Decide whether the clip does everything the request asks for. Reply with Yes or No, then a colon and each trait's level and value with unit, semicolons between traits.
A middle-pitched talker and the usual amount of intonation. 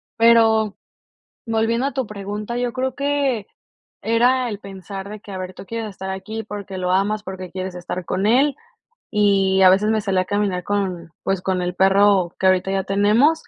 No: high, 205 Hz; average, 3.0 semitones